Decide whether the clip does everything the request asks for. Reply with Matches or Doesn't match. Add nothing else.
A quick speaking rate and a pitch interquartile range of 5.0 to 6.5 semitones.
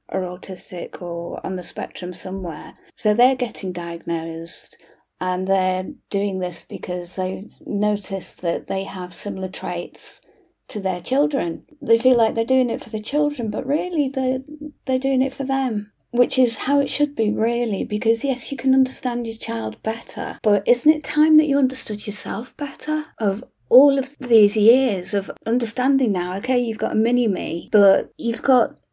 Doesn't match